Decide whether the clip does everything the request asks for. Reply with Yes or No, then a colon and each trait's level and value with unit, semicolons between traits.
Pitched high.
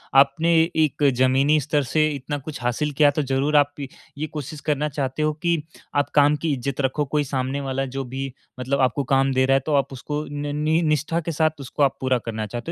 No: medium, 140 Hz